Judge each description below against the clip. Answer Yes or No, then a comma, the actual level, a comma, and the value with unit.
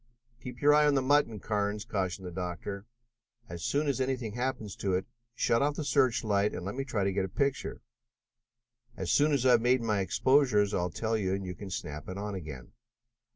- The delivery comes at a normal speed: No, fast, 215 wpm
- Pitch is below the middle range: Yes, low, 105 Hz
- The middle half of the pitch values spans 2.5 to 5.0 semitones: No, wide, 5.4 semitones